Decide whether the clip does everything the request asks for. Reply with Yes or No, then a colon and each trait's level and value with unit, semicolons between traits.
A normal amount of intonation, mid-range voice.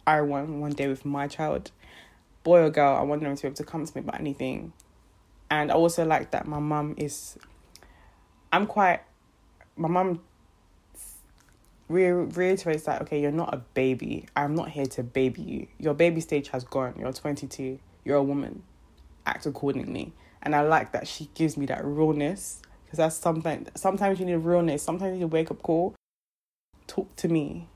Yes: average, 3.4 semitones; medium, 150 Hz